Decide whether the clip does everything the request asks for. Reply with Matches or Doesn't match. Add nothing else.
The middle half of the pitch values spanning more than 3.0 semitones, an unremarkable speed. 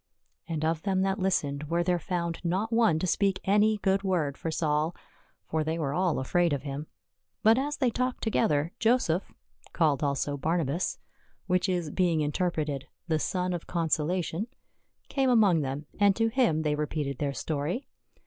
Matches